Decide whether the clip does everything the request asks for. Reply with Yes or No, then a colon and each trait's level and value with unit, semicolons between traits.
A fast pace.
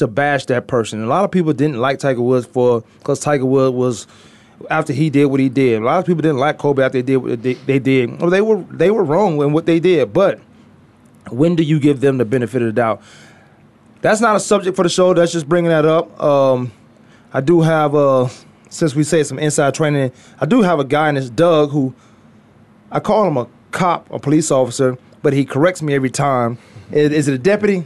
Yes: fast, 235 wpm